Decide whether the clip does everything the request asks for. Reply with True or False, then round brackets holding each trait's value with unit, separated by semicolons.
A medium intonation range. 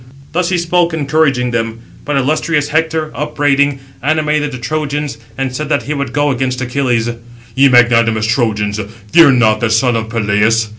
True (4.6 semitones)